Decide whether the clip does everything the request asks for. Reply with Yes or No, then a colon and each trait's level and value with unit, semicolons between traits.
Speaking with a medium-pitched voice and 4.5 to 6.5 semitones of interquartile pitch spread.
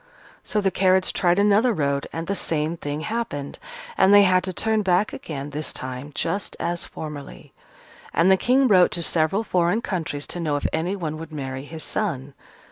Yes: medium, 170 Hz; average, 4.9 semitones